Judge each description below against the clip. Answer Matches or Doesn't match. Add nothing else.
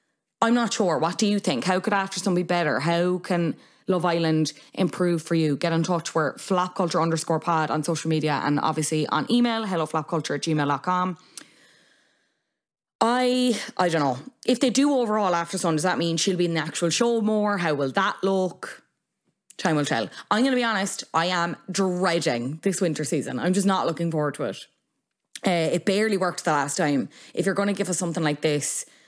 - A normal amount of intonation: Matches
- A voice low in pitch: Doesn't match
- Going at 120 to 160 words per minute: Doesn't match